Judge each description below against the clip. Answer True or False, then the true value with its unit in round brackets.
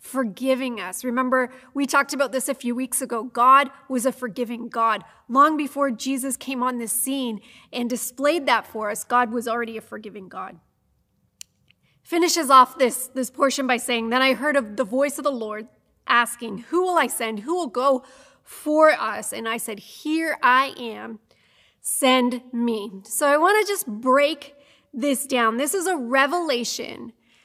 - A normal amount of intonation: True (3.0 semitones)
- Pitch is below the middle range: False (255 Hz)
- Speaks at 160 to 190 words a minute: True (175 wpm)